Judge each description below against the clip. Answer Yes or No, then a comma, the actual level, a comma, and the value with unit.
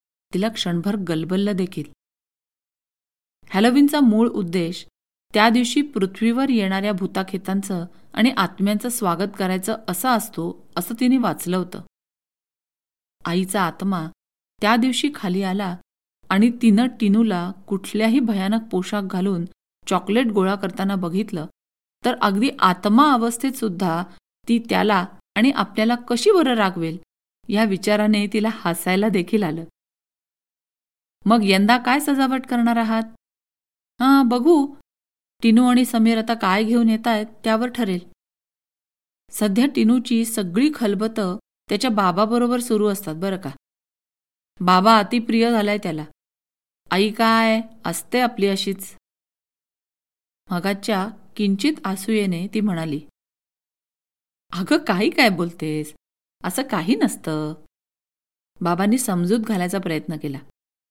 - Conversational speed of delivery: Yes, average, 110 wpm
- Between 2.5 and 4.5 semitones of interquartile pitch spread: Yes, average, 4.2 semitones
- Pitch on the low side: No, high, 205 Hz